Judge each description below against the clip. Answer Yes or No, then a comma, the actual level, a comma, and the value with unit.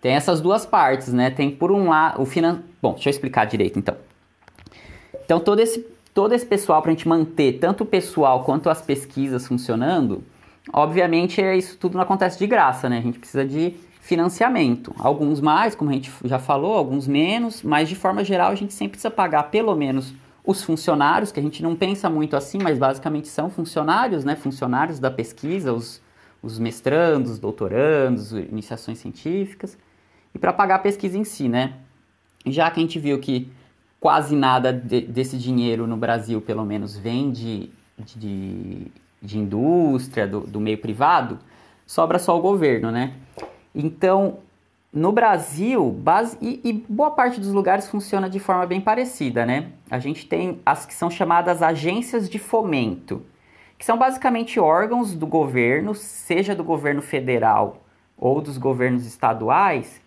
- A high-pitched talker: No, medium, 155 Hz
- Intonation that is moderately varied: No, wide, 6.9 semitones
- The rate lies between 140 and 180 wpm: Yes, average, 170 wpm